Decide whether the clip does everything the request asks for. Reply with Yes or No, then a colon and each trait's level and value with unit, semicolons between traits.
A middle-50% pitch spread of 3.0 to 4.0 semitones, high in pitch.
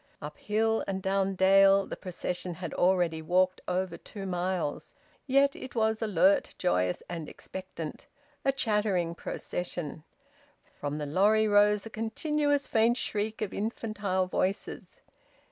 Yes: average, 3.4 semitones; high, 195 Hz